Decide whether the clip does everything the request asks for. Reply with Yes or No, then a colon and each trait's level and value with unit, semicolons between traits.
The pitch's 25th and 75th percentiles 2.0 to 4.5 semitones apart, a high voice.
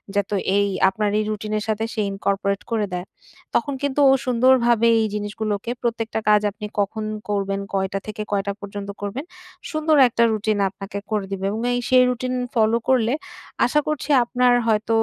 Yes: average, 2.9 semitones; high, 215 Hz